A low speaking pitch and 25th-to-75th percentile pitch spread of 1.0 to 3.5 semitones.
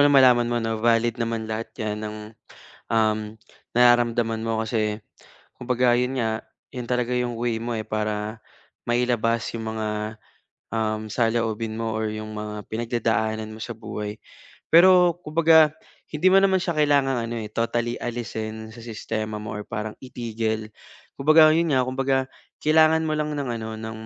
Yes: low, 115 Hz; narrow, 2.6 semitones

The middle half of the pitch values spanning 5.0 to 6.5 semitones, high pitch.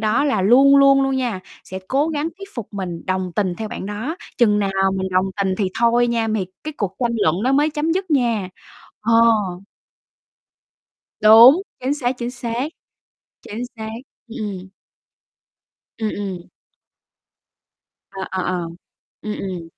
Yes: wide, 5.6 semitones; high, 225 Hz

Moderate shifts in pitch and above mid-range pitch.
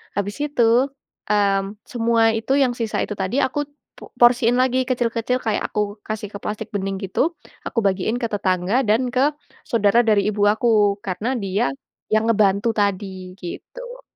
Yes: average, 3.2 semitones; high, 215 Hz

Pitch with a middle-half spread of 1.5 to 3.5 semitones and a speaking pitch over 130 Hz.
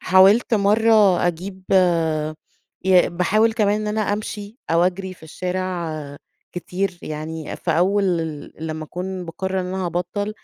Yes: average, 2.7 semitones; medium, 185 Hz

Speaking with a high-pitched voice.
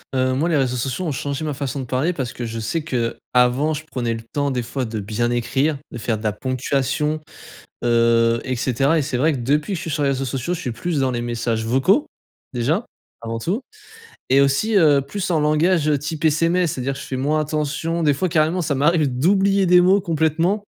No: medium, 140 Hz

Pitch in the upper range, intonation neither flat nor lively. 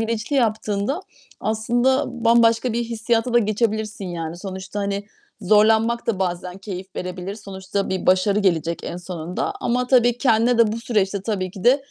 Yes: high, 215 Hz; average, 3.5 semitones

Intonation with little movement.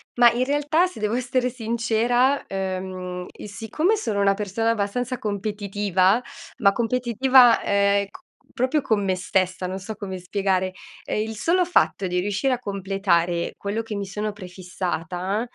No: average, 4.1 semitones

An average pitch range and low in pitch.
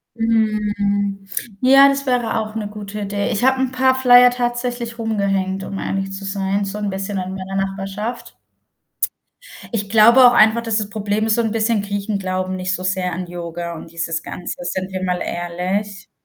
No: average, 3.0 semitones; high, 205 Hz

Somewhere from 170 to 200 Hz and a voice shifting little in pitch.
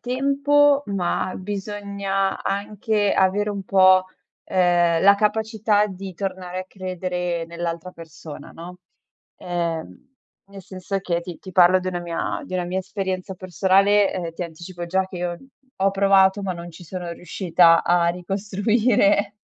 Yes: medium, 185 Hz; narrow, 2.3 semitones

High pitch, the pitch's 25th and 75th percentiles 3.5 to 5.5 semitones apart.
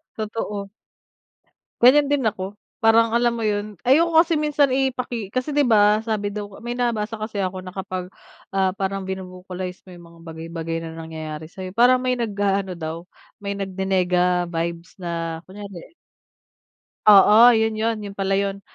Yes: high, 200 Hz; average, 3.8 semitones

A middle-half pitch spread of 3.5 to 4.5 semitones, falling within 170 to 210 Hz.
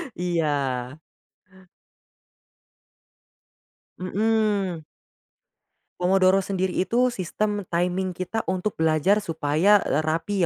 Yes: average, 3.9 semitones; medium, 185 Hz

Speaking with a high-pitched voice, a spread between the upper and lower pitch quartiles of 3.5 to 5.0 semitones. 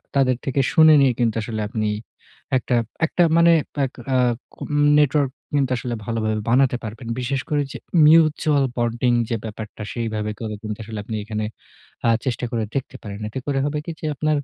No: low, 125 Hz; average, 4.1 semitones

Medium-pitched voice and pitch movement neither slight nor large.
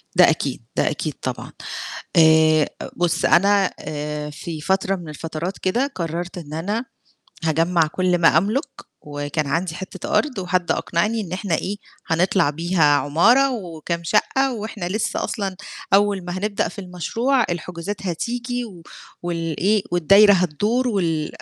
Yes: medium, 180 Hz; average, 4.1 semitones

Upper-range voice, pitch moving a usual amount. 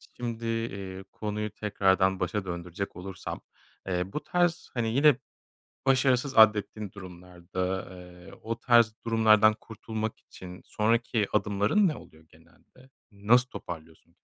No: low, 105 Hz; average, 3.7 semitones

